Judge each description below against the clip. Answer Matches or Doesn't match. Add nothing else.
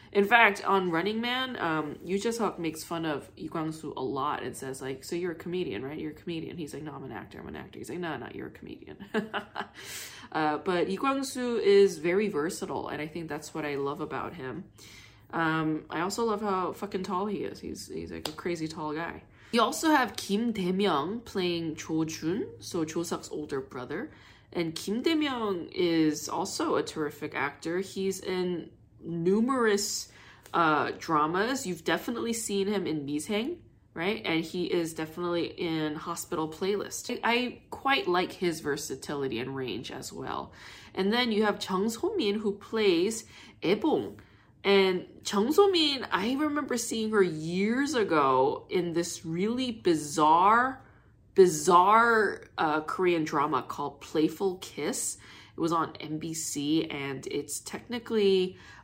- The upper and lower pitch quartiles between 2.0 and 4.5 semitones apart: Doesn't match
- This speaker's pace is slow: Doesn't match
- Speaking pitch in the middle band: Matches